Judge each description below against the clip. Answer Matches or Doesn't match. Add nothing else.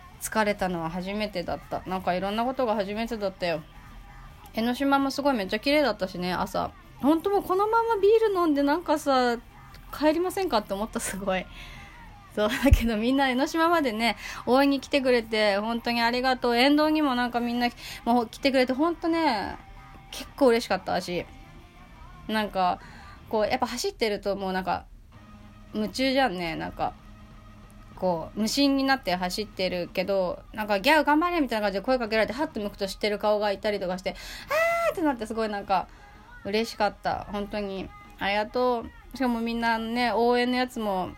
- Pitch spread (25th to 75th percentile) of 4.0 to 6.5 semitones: Matches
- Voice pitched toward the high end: Matches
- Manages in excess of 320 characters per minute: Matches